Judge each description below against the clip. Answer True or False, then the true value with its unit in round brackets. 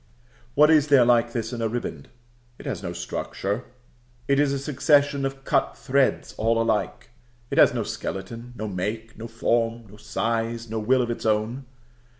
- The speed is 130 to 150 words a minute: False (175 wpm)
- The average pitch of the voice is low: True (115 Hz)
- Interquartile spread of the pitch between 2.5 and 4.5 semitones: True (3.3 semitones)